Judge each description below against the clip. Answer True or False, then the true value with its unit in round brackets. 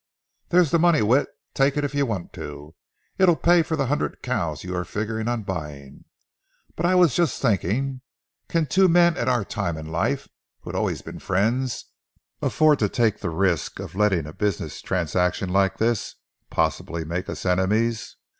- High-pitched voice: False (110 Hz)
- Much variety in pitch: True (7.8 semitones)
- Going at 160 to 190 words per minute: True (180 wpm)